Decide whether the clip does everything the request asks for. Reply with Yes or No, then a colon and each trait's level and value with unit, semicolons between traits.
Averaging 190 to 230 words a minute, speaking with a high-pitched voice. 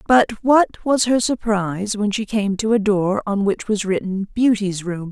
Yes: average, 200 wpm; high, 210 Hz